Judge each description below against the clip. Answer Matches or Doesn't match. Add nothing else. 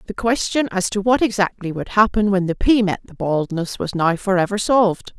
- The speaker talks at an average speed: Doesn't match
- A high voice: Matches